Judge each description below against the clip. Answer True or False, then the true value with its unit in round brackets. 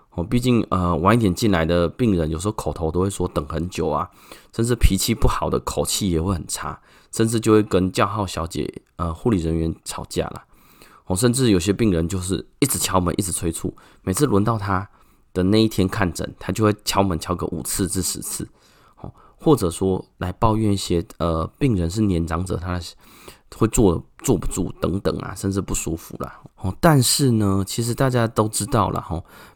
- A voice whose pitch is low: True (95 Hz)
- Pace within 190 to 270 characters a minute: False (280 characters per minute)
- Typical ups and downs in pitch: True (3.9 semitones)